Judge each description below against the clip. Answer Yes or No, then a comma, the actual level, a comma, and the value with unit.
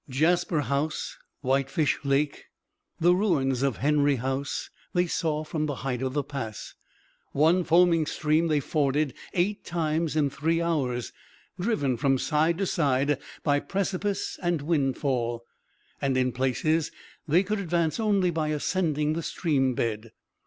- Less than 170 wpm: Yes, average, 140 wpm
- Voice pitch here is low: No, medium, 150 Hz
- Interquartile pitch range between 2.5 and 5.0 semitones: Yes, average, 3.8 semitones